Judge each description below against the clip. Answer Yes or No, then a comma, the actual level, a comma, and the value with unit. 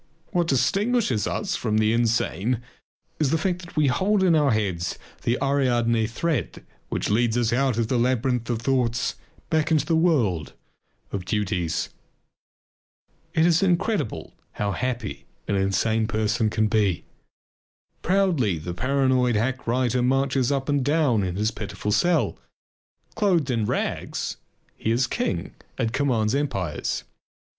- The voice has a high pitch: No, low, 125 Hz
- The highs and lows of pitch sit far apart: No, average, 4.8 semitones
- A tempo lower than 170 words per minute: Yes, average, 140 wpm